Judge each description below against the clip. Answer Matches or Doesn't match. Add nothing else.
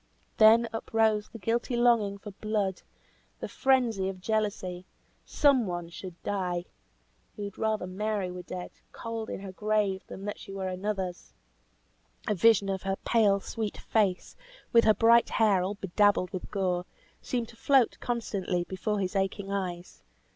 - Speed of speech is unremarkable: Matches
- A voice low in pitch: Doesn't match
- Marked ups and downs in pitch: Doesn't match